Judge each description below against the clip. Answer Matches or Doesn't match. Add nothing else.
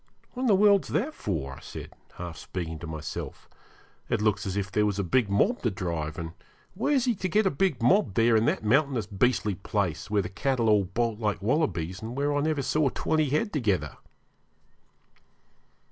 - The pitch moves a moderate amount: Doesn't match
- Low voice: Matches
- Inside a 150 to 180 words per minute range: Doesn't match